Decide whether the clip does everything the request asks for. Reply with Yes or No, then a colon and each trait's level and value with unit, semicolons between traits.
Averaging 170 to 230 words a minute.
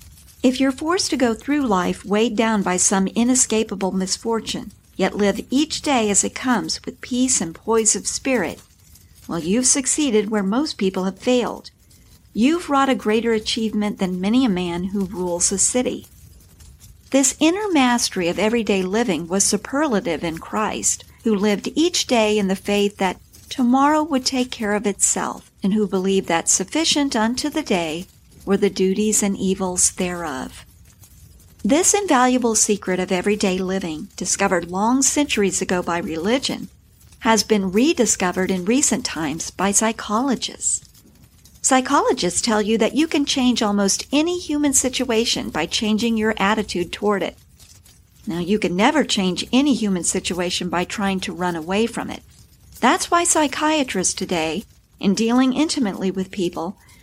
No: average, 155 wpm